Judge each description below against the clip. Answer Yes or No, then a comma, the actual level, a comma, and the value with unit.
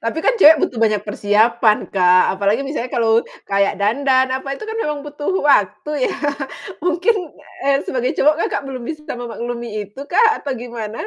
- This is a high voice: Yes, high, 245 Hz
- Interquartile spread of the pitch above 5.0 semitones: Yes, wide, 5.4 semitones